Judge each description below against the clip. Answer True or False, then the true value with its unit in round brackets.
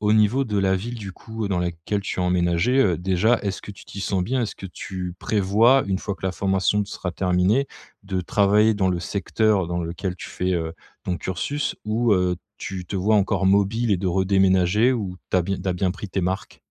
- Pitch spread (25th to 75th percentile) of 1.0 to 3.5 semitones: True (2.6 semitones)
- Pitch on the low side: True (95 Hz)